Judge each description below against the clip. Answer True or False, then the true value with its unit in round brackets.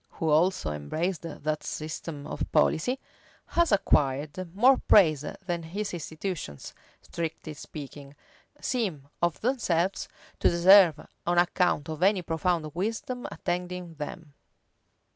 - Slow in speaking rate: True (115 wpm)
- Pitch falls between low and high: True (170 Hz)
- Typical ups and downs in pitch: True (3.5 semitones)